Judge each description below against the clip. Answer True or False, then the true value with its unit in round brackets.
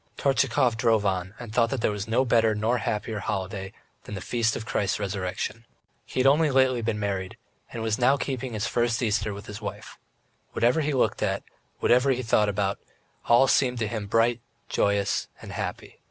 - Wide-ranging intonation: False (3.2 semitones)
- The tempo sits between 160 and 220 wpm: True (195 wpm)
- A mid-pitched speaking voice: False (115 Hz)